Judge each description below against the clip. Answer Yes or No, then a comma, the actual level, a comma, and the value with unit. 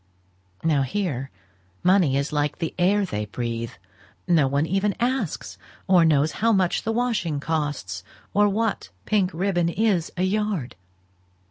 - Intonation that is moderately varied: No, wide, 6.1 semitones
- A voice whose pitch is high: No, medium, 170 Hz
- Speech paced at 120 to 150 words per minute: Yes, average, 140 wpm